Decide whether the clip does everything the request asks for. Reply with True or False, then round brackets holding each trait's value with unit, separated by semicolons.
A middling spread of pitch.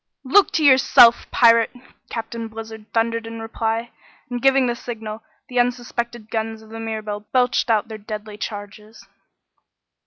False (1.7 semitones)